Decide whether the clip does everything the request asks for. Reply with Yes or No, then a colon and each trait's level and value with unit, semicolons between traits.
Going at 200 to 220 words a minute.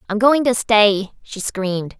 No: average, 180 wpm